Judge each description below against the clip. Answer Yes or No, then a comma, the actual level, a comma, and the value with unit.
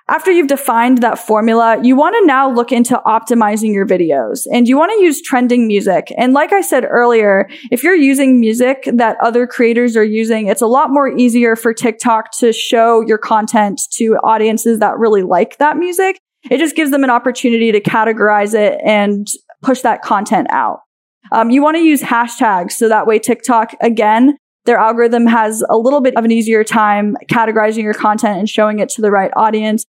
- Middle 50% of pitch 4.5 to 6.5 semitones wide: No, average, 2.9 semitones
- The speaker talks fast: No, average, 195 wpm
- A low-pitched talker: No, high, 230 Hz